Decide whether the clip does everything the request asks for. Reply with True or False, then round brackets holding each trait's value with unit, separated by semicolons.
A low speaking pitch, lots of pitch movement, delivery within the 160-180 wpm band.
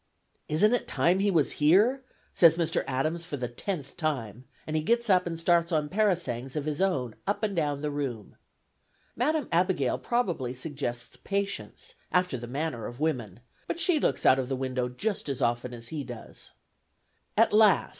False (155 Hz; 6.8 semitones; 175 wpm)